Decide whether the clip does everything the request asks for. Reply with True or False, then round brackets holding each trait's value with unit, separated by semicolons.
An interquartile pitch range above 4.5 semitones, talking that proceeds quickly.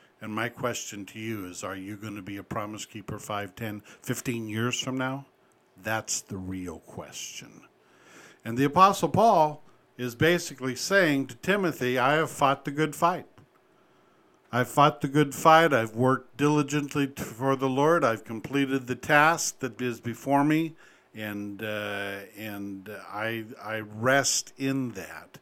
False (5.3 semitones; 155 wpm)